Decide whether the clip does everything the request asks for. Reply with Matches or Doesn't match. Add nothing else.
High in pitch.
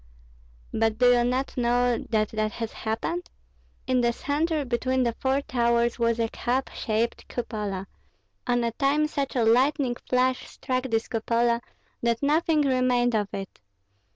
Matches